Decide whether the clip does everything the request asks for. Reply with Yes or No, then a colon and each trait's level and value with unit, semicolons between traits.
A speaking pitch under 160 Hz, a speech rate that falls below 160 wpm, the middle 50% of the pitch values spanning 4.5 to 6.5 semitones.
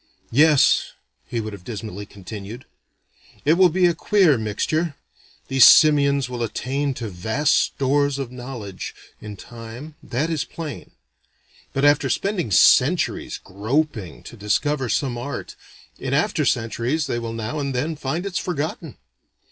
Yes: low, 135 Hz; average, 140 wpm; average, 5.0 semitones